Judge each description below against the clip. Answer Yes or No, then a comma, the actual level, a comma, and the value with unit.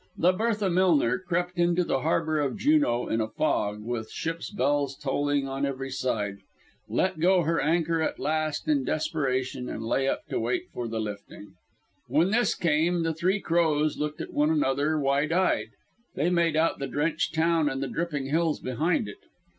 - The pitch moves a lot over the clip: No, average, 4.1 semitones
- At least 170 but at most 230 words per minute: Yes, average, 180 wpm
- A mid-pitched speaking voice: Yes, medium, 155 Hz